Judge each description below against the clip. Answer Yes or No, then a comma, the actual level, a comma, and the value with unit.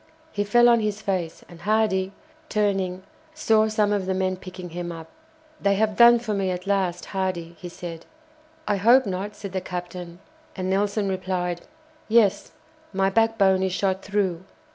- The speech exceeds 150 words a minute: Yes, average, 165 wpm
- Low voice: No, high, 190 Hz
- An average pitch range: No, narrow, 2.3 semitones